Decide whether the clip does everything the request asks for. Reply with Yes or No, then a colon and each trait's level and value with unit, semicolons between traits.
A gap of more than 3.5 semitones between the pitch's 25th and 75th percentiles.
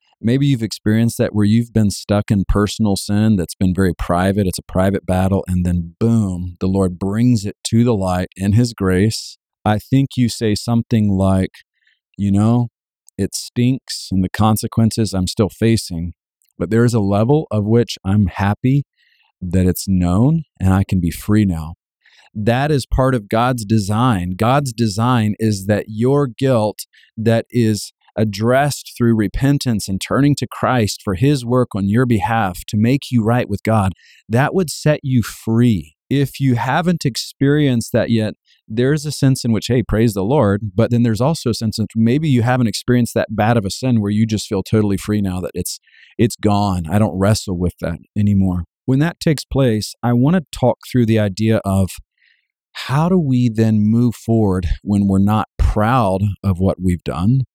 Yes: average, 3.9 semitones